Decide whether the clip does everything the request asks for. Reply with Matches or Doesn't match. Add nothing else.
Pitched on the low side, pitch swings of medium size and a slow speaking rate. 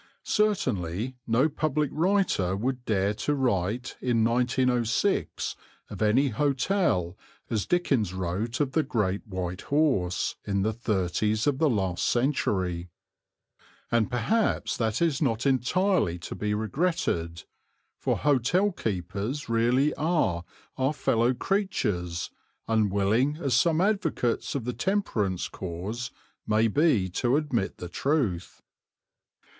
Doesn't match